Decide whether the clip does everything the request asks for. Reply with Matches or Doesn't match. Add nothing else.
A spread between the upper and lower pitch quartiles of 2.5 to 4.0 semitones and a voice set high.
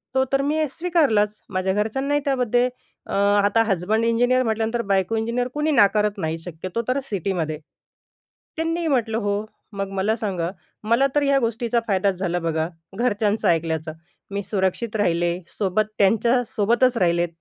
Doesn't match